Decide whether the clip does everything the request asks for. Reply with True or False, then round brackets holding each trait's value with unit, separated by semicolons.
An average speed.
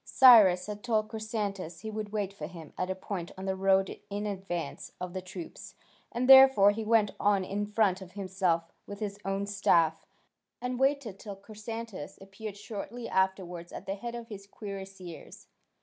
True (170 wpm)